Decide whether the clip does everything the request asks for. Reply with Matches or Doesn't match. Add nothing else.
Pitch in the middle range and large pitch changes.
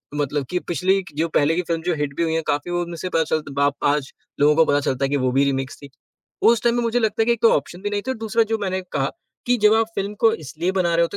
Matches